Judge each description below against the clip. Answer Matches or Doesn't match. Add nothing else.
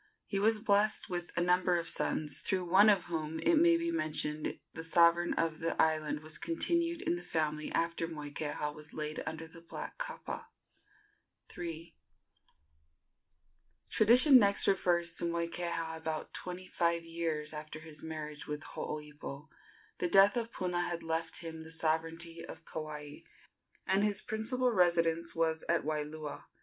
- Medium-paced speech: Matches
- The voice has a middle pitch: Matches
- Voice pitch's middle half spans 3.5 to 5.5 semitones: Doesn't match